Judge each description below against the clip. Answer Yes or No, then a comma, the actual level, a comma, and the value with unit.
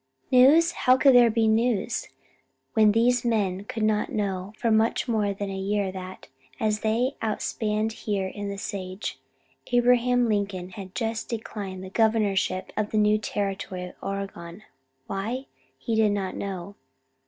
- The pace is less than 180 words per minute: Yes, average, 155 wpm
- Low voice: No, high, 210 Hz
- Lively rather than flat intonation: No, average, 2.7 semitones